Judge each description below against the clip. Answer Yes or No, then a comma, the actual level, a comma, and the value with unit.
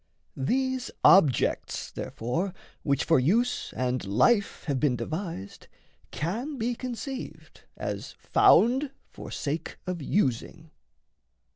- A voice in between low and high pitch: Yes, medium, 170 Hz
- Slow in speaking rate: Yes, slow, 105 wpm